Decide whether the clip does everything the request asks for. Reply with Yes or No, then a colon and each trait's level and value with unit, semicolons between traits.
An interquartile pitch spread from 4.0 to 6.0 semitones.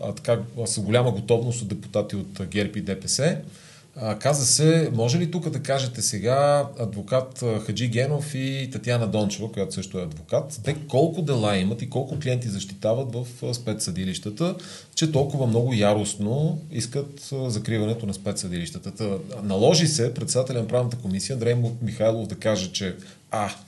Yes: average, 4.7 semitones